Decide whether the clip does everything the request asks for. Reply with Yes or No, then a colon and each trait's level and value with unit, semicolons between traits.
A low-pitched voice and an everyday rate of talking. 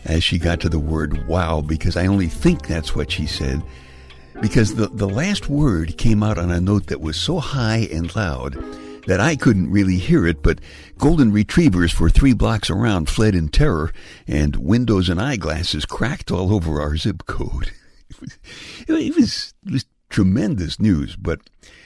Yes: very low, 90 Hz; average, 175 wpm